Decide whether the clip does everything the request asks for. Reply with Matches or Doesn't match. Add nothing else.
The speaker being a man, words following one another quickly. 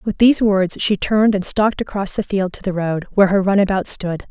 Doesn't match